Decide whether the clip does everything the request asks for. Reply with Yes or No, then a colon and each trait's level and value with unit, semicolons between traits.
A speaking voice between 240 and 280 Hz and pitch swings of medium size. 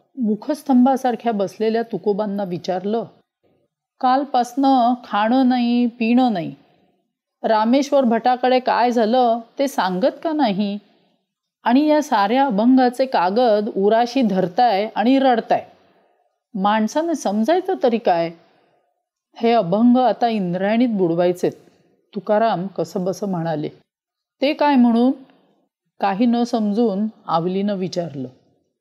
No: high, 225 Hz; average, 4.5 semitones